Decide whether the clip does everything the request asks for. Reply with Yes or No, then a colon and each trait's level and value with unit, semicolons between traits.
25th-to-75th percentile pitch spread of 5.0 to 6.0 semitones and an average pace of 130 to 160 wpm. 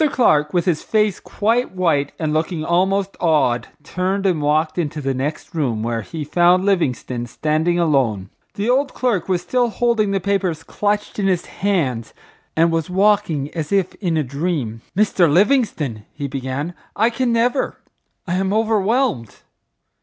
Yes: wide, 5.4 semitones; average, 155 wpm